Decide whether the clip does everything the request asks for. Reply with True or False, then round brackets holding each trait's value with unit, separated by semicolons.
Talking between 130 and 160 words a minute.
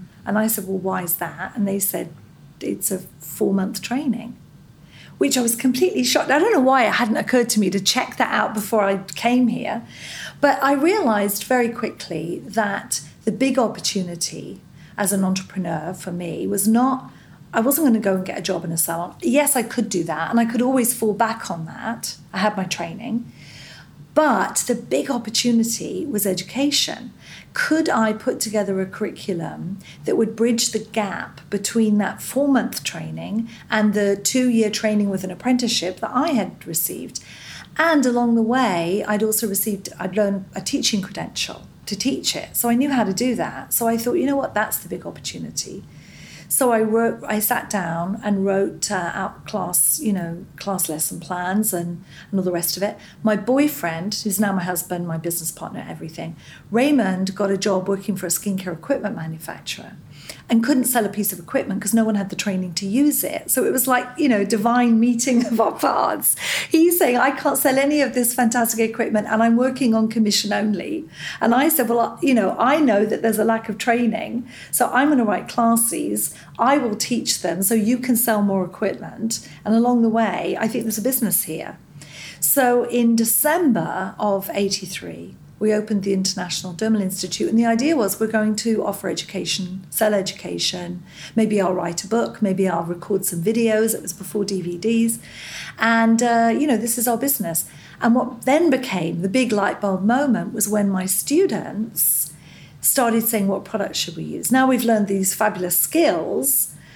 False (190 wpm)